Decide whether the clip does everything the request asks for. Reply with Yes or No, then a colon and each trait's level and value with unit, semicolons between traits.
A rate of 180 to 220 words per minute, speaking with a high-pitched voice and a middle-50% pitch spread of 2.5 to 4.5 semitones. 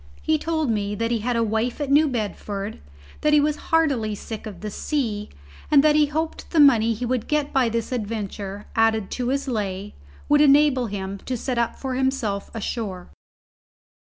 No: average, 190 wpm; high, 235 Hz; average, 5.1 semitones